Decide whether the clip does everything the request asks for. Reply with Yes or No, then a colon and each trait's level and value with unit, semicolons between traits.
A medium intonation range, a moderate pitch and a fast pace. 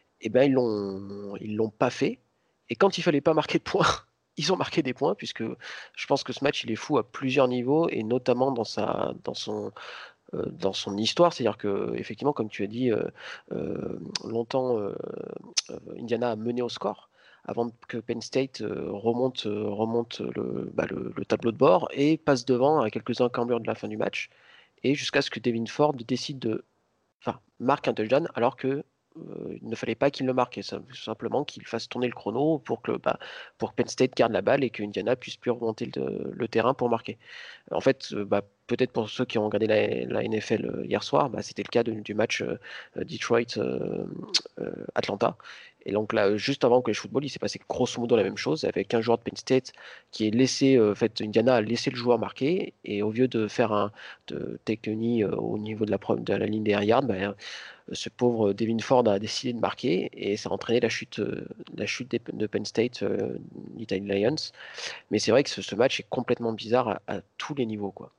No: average, 3.1 semitones; low, 115 Hz; fast, 225 wpm